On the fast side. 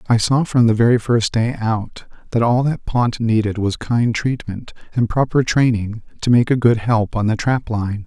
Yes: fast, 210 wpm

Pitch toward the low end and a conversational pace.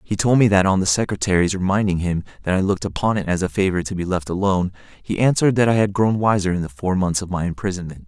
No: very low, 95 Hz; fast, 260 wpm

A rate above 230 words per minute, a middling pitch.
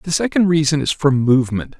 No: average, 200 wpm; medium, 150 Hz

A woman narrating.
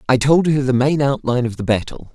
No: male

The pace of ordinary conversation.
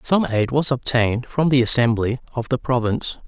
Yes: average, 185 wpm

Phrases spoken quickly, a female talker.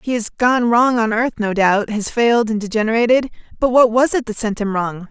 Yes: fast, 225 wpm; female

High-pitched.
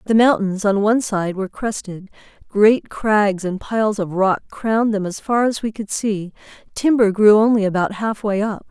Yes: high, 210 Hz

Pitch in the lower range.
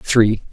Yes: low, 110 Hz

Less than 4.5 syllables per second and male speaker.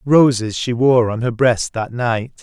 Yes: 3.9 syllables/s; male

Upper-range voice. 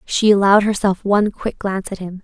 Yes: high, 200 Hz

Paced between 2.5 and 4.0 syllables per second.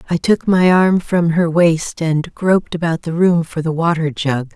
No: 4.4 syllables/s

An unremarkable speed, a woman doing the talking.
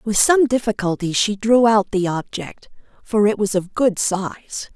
Yes: average, 175 wpm; female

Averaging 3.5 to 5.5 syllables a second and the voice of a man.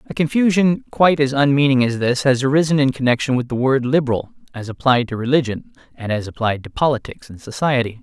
No: 6.1 syllables/s; male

